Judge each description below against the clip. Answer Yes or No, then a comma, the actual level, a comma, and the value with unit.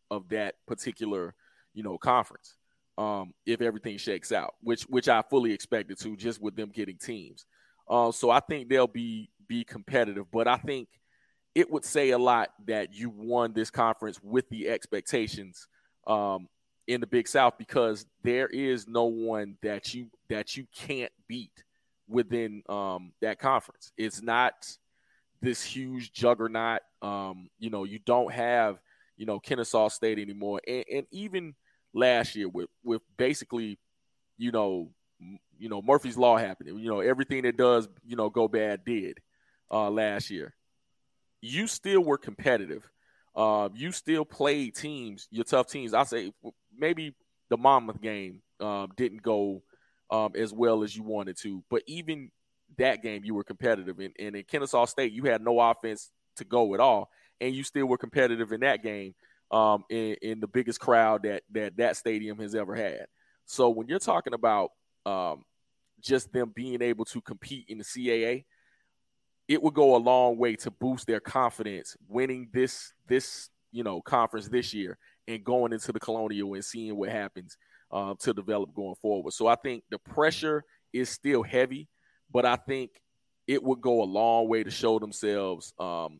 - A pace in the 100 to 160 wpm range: No, average, 175 wpm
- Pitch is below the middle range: Yes, low, 115 Hz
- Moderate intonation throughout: Yes, average, 3.0 semitones